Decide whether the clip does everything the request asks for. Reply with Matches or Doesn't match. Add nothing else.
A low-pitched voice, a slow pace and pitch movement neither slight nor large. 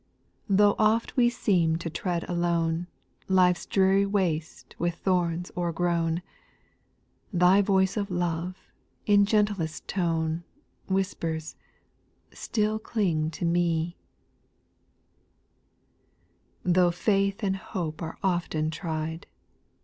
Doesn't match